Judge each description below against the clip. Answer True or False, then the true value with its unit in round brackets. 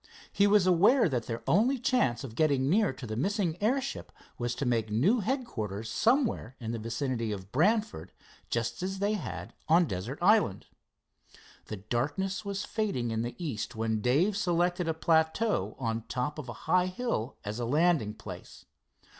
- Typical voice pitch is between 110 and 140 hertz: False (150 Hz)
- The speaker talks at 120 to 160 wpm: False (170 wpm)